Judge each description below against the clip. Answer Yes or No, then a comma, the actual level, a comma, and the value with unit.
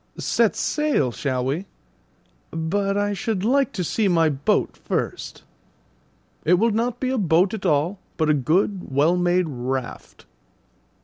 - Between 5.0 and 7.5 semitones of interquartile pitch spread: Yes, average, 5.3 semitones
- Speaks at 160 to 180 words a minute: No, average, 145 wpm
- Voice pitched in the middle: Yes, medium, 180 Hz